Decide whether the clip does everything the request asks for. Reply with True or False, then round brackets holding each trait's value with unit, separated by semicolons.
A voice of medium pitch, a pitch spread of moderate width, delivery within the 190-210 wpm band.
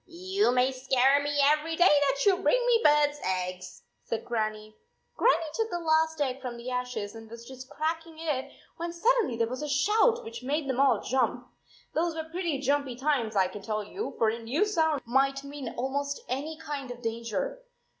False (275 Hz; 4.9 semitones; 200 wpm)